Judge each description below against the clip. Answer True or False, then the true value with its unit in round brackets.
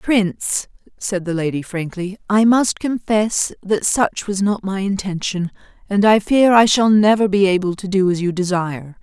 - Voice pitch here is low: False (195 Hz)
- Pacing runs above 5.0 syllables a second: False (4.5 syllables/s)